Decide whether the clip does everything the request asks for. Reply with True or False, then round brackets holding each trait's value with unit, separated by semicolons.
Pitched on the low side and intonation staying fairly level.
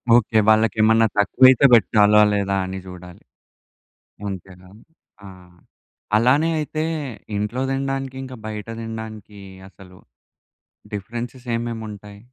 False (110 Hz; 3.2 semitones)